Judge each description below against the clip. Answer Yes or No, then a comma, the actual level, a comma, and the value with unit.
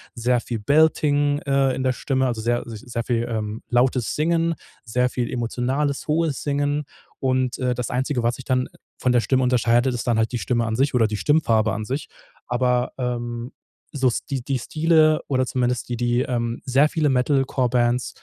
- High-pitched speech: No, low, 125 Hz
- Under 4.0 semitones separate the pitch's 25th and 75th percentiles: Yes, narrow, 2.4 semitones